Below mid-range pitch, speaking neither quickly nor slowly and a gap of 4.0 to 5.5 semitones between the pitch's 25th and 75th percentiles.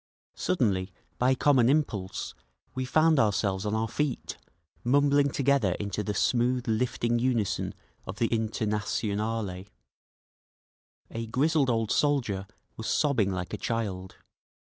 No: low, 115 Hz; slow, 120 wpm; average, 4.3 semitones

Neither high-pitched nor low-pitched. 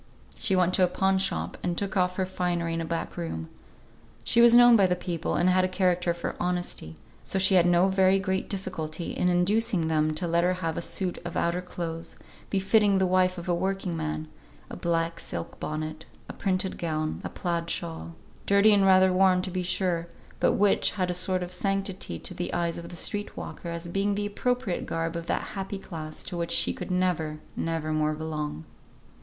Yes: medium, 180 Hz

